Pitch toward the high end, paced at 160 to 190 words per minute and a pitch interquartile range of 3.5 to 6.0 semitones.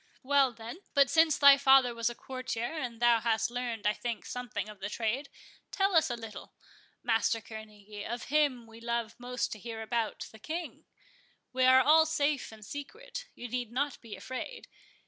Yes: high, 240 Hz; average, 180 wpm; average, 3.8 semitones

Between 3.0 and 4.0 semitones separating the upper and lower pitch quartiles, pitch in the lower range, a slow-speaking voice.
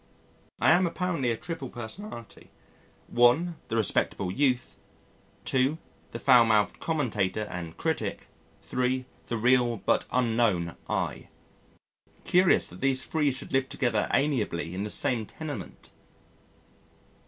No: average, 4.4 semitones; low, 125 Hz; slow, 120 wpm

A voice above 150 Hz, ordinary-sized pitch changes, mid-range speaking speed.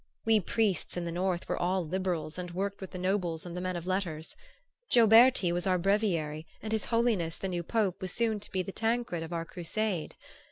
No: medium, 185 Hz; average, 3.4 semitones; fast, 210 wpm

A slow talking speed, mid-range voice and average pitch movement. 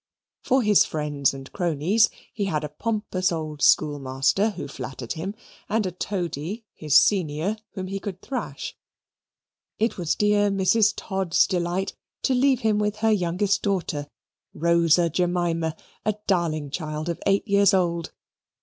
No: average, 145 wpm; medium, 180 Hz; average, 4.8 semitones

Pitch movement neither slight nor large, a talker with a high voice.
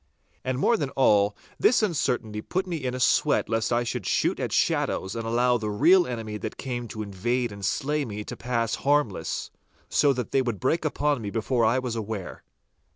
No: average, 3.9 semitones; low, 120 Hz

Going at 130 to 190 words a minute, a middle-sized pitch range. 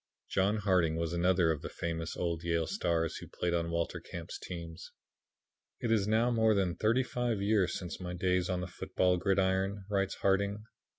Yes: average, 180 wpm; average, 3.0 semitones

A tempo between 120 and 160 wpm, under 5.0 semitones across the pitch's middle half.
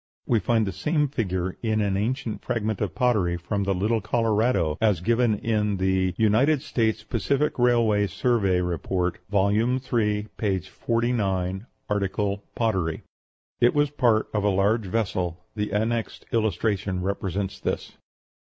Yes: average, 140 wpm; average, 3.3 semitones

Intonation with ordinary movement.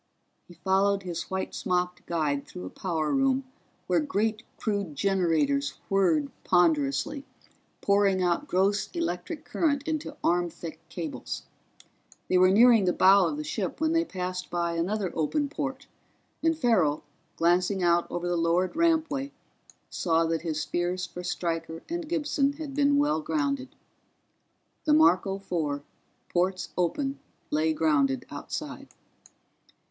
No: wide, 8.4 semitones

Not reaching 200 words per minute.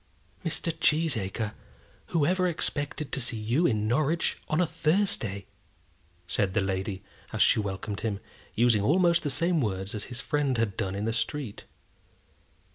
Yes: average, 150 wpm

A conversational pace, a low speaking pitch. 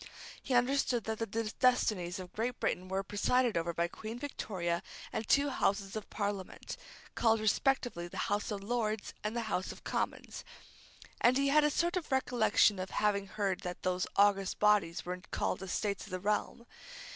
No: average, 175 wpm; high, 210 Hz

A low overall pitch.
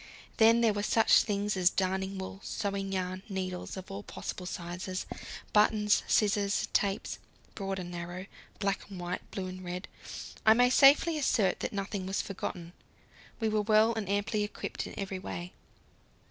No: high, 195 Hz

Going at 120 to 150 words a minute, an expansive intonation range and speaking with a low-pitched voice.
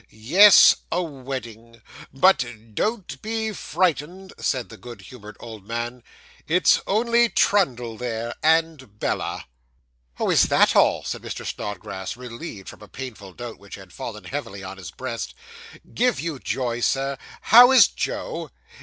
Yes: average, 145 wpm; wide, 7.4 semitones; low, 125 Hz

